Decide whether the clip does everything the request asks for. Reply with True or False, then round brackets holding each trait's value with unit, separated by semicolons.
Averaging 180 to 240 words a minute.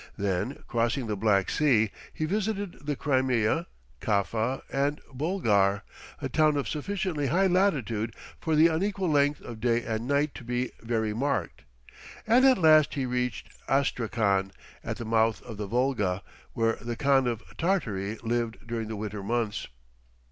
False (155 wpm)